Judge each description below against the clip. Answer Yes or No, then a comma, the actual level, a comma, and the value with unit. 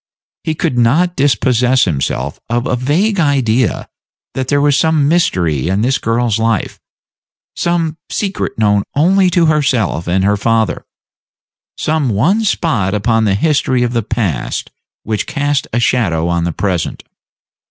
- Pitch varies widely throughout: Yes, wide, 6.5 semitones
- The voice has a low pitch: Yes, low, 120 Hz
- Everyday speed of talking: Yes, average, 145 wpm